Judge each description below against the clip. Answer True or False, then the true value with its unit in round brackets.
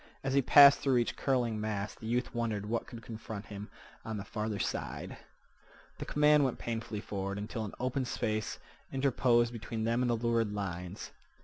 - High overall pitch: False (115 Hz)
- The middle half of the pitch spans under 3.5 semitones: True (2.7 semitones)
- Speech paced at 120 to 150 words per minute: False (180 wpm)